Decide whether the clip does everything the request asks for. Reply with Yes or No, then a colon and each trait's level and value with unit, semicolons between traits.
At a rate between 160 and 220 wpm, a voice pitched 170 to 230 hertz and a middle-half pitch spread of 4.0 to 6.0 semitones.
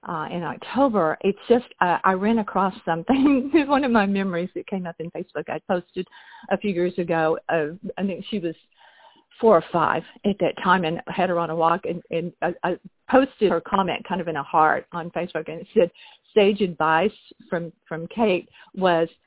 Yes: average, 200 wpm; medium, 185 Hz; average, 4.5 semitones